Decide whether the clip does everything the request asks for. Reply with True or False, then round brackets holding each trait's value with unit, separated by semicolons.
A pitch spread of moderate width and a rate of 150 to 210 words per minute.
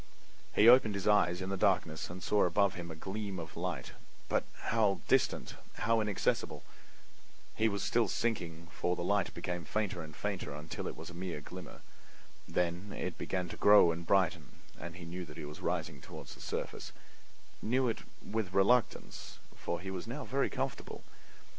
True (3.7 semitones; 175 wpm)